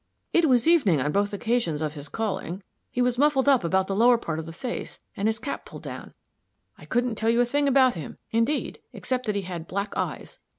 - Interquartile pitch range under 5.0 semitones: No, average, 5.3 semitones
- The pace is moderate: No, fast, 225 wpm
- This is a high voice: Yes, high, 225 Hz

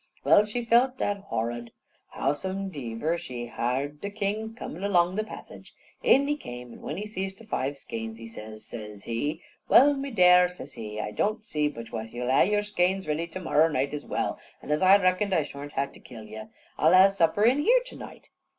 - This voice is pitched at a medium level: Yes, medium, 170 Hz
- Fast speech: Yes, fast, 215 wpm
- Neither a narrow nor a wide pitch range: No, wide, 8.7 semitones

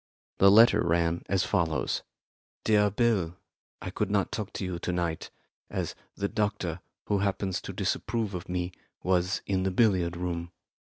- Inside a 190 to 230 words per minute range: No, average, 160 wpm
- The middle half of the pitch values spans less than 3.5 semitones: Yes, average, 2.8 semitones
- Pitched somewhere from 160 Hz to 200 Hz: No, very low, 95 Hz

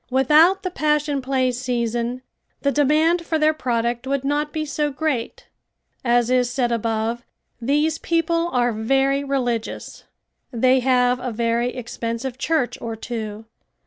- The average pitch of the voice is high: Yes, very high, 255 Hz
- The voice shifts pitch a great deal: No, average, 3.7 semitones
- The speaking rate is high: No, average, 140 wpm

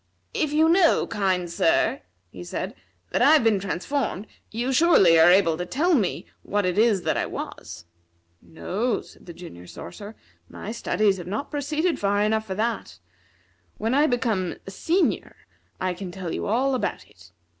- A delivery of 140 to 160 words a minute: No, average, 175 wpm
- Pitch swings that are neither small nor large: No, wide, 6.4 semitones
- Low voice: No, high, 210 Hz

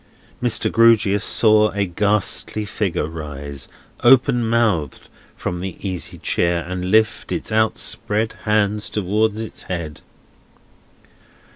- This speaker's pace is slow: Yes, slow, 110 wpm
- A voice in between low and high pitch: No, low, 105 Hz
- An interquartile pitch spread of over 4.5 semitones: No, average, 3.7 semitones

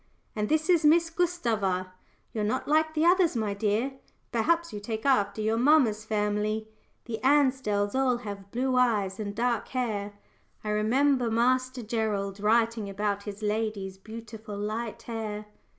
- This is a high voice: Yes, high, 220 Hz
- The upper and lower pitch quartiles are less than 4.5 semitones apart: Yes, average, 3.7 semitones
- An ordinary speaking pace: Yes, average, 150 wpm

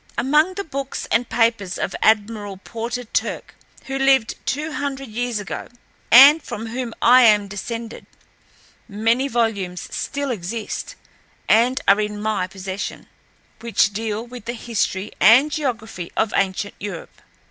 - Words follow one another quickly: No, slow, 135 wpm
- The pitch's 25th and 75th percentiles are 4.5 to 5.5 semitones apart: No, average, 3.6 semitones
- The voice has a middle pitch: No, high, 230 Hz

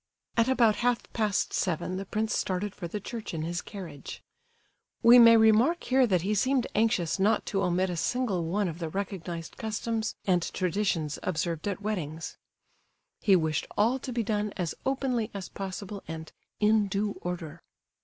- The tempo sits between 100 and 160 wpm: No, average, 170 wpm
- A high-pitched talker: Yes, high, 200 Hz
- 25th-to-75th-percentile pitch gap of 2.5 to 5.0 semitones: Yes, average, 4.0 semitones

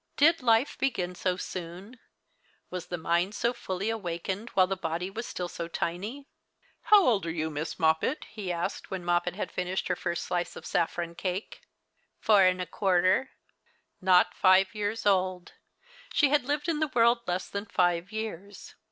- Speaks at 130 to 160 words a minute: No, average, 180 wpm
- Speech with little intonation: No, average, 4.0 semitones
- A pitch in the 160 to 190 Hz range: Yes, medium, 185 Hz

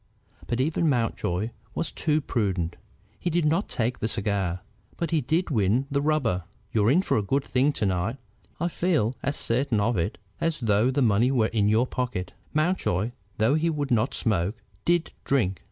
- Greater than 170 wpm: Yes, average, 185 wpm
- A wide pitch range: Yes, wide, 6.3 semitones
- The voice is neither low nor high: No, low, 120 Hz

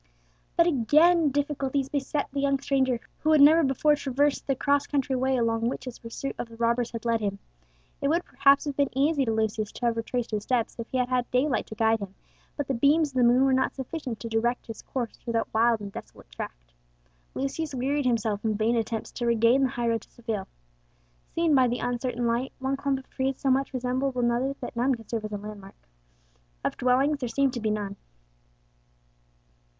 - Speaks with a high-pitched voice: Yes, very high, 250 Hz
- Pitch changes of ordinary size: Yes, average, 3.2 semitones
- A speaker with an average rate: No, fast, 210 wpm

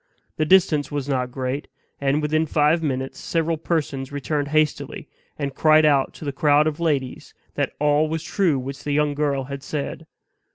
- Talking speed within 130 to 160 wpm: No, average, 175 wpm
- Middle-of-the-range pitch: Yes, medium, 145 Hz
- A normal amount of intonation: No, narrow, 2.0 semitones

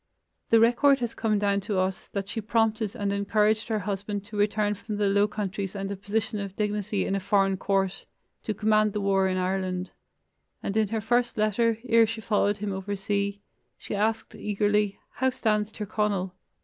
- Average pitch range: No, narrow, 1.6 semitones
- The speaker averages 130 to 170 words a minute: No, average, 190 wpm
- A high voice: Yes, high, 205 Hz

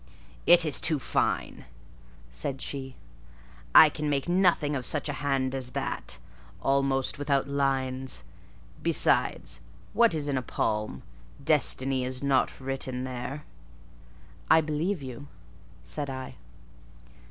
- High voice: No, low, 135 Hz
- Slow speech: Yes, slow, 120 wpm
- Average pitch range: No, narrow, 2.2 semitones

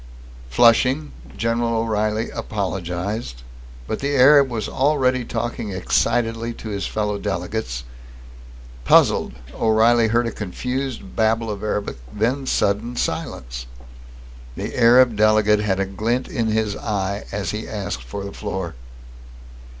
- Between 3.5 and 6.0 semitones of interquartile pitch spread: No, average, 2.8 semitones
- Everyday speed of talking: No, slow, 125 wpm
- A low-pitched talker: Yes, low, 110 Hz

